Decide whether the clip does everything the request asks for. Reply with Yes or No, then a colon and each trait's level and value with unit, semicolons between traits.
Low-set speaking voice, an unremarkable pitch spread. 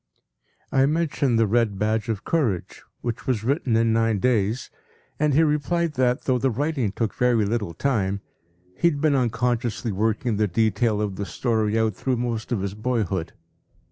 Yes: low, 115 Hz; average, 3.5 semitones